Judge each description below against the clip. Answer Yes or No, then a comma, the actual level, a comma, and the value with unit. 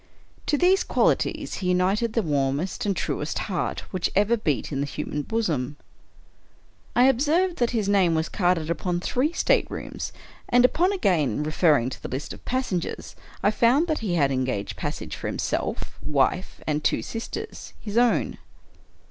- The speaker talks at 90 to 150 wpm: No, average, 165 wpm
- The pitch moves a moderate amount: No, wide, 8.1 semitones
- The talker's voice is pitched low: No, medium, 185 Hz